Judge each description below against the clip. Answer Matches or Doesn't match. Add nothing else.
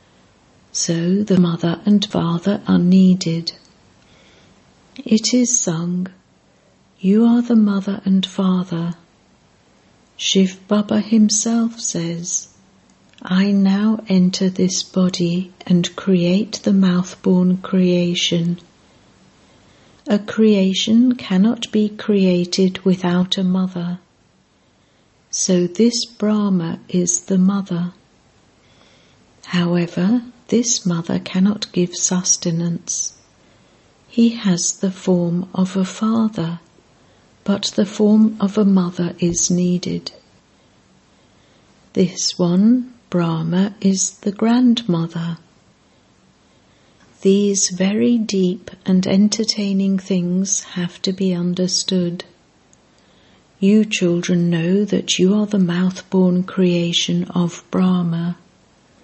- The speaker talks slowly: Matches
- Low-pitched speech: Doesn't match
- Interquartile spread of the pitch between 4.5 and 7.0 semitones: Doesn't match